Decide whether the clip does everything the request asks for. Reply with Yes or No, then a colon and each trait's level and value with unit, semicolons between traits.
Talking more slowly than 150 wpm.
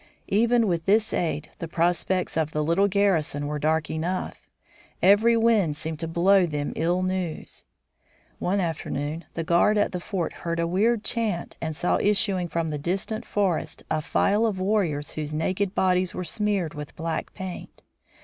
No: average, 170 wpm